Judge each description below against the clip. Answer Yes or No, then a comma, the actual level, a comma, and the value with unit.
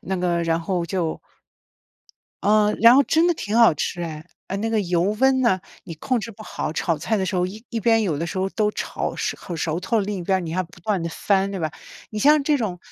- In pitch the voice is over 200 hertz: No, high, 195 Hz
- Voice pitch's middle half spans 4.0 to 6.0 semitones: Yes, average, 4.4 semitones